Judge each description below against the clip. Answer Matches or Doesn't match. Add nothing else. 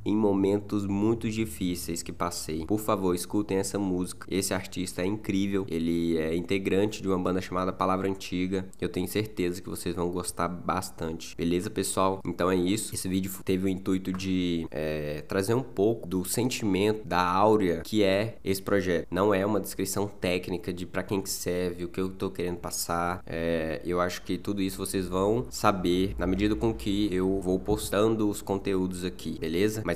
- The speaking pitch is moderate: Doesn't match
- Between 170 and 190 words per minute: Matches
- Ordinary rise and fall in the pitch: Doesn't match